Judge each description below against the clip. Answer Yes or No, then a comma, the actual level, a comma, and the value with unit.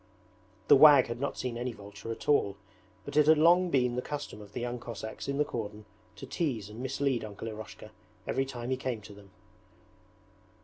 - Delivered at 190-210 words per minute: Yes, average, 195 wpm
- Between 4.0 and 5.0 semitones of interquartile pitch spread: Yes, average, 4.3 semitones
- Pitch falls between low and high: No, low, 120 Hz